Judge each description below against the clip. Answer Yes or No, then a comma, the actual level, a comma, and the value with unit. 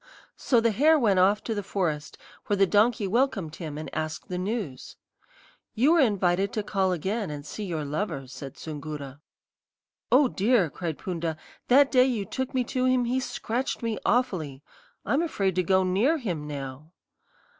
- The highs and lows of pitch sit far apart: Yes, wide, 7.4 semitones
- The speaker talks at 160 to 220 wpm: Yes, average, 175 wpm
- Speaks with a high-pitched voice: Yes, high, 195 Hz